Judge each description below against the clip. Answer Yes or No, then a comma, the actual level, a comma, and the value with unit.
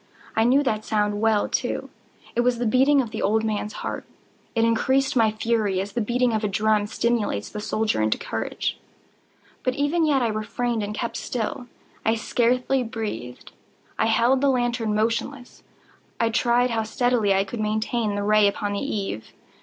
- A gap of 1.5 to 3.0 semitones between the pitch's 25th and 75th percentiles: Yes, narrow, 2.5 semitones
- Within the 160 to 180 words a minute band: Yes, average, 175 wpm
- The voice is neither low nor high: No, high, 225 Hz